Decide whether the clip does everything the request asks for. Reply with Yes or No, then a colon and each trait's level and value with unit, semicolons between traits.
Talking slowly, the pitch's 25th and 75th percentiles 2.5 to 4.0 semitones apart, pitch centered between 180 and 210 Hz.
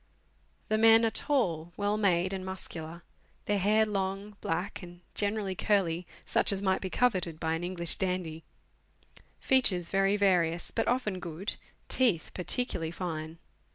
No: average, 145 wpm; average, 3.4 semitones; high, 190 Hz